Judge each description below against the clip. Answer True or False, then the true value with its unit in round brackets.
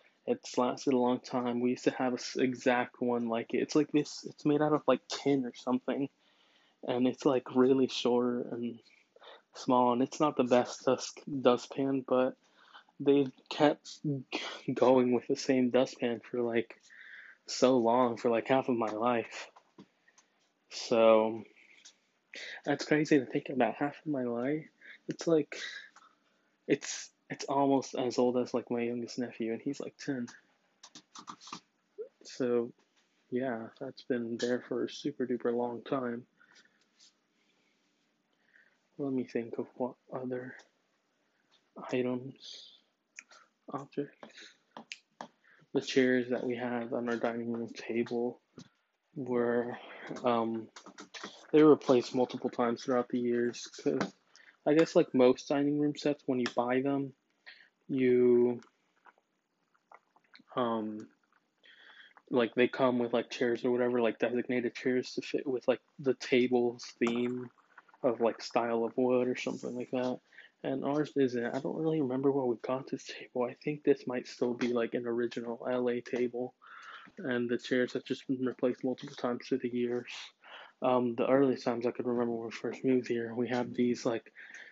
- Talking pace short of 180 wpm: True (150 wpm)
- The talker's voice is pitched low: True (125 Hz)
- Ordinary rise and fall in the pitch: False (1.7 semitones)